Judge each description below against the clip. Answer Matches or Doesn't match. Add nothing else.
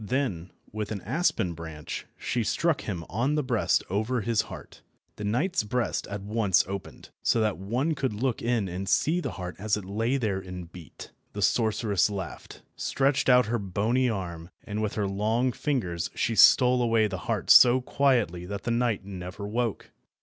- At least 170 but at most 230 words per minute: Matches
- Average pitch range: Matches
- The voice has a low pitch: Matches